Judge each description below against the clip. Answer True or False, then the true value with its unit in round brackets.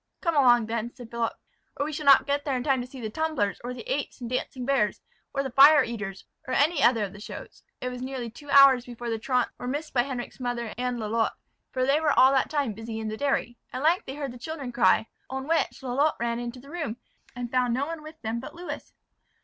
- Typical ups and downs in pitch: True (3.1 semitones)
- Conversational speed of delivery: False (245 wpm)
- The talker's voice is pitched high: True (255 Hz)